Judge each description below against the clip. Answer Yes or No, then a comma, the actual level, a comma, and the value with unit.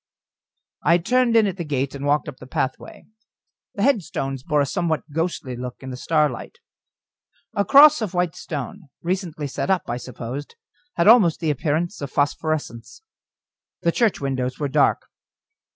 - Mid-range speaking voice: Yes, medium, 155 Hz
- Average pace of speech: Yes, average, 160 wpm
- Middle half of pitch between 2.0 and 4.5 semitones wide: No, average, 5.0 semitones